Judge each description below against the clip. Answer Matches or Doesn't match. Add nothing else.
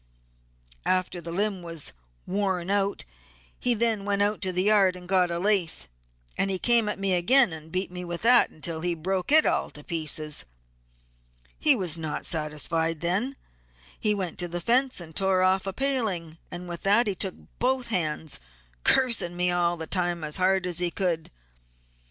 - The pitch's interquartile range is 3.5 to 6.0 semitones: Doesn't match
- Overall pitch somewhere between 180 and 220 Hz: Matches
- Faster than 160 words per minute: Matches